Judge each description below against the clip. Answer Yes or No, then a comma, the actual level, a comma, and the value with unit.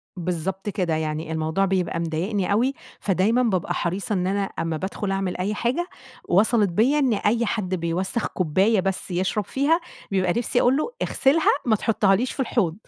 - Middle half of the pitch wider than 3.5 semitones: Yes, average, 4.2 semitones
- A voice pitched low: No, high, 195 Hz